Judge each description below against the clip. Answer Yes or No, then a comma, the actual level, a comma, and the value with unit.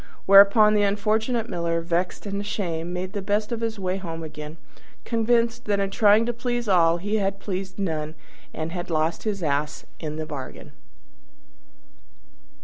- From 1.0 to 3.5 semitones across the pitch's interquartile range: No, average, 4.3 semitones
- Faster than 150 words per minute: Yes, average, 160 wpm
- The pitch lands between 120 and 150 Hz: No, high, 195 Hz